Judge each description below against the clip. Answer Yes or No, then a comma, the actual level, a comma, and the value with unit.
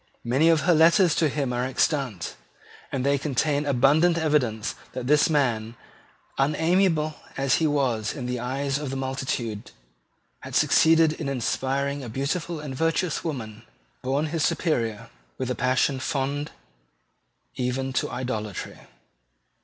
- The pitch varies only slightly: No, average, 3.5 semitones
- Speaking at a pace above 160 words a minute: No, average, 140 wpm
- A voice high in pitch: No, low, 135 Hz